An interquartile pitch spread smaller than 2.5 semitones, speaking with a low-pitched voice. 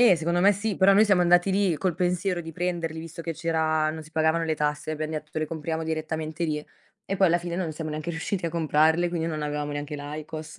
No: narrow, 2.1 semitones; medium, 160 Hz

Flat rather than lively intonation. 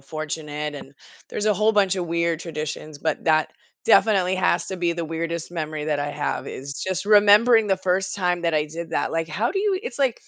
No: average, 4.4 semitones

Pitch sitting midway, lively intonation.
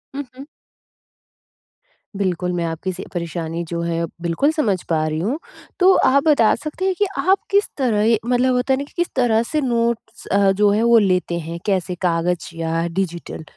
No: high, 205 Hz; wide, 7.2 semitones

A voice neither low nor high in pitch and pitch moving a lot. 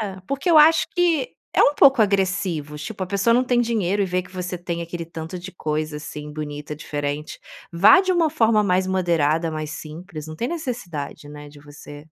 Yes: medium, 180 Hz; wide, 6.5 semitones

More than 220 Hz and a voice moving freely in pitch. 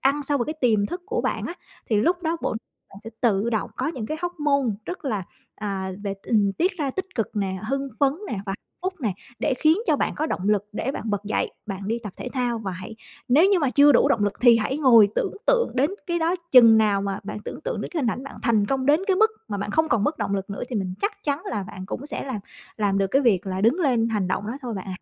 Yes: high, 235 Hz; wide, 6.1 semitones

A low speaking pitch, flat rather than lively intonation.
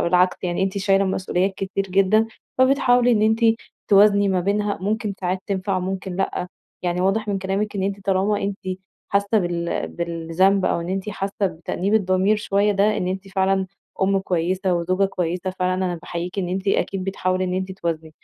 No: high, 190 Hz; narrow, 1.6 semitones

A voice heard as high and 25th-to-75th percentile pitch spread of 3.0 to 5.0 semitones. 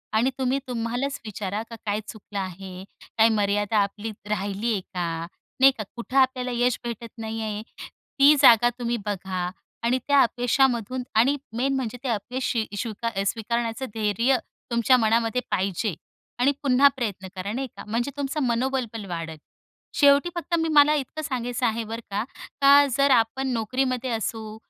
Yes: high, 235 Hz; average, 3.7 semitones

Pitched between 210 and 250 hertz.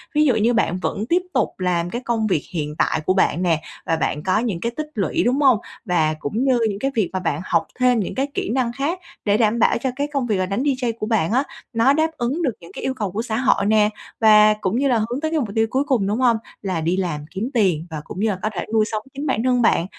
Yes: high, 220 Hz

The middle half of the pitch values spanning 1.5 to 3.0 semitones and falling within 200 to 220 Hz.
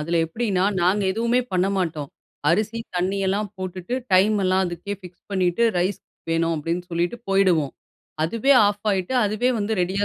No: average, 2.7 semitones; medium, 185 Hz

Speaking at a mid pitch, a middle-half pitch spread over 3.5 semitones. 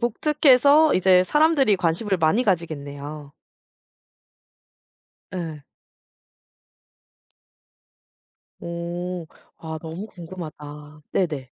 Yes: medium, 175 Hz; average, 5.2 semitones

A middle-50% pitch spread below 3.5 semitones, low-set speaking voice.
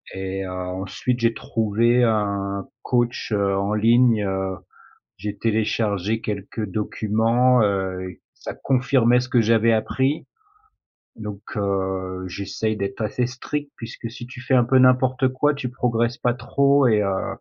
No: average, 3.8 semitones; low, 110 Hz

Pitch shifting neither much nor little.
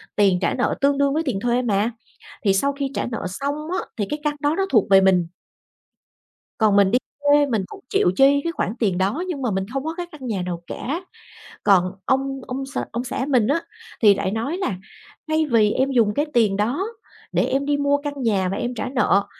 No: wide, 5.9 semitones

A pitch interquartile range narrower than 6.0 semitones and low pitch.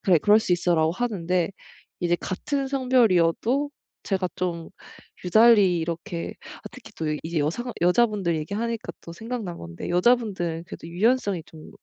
No: wide, 5.4 semitones; medium, 185 Hz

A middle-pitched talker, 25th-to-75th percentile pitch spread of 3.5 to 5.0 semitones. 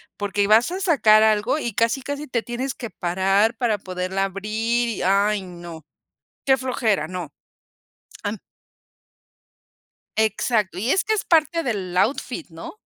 No: high, 215 Hz; average, 4.7 semitones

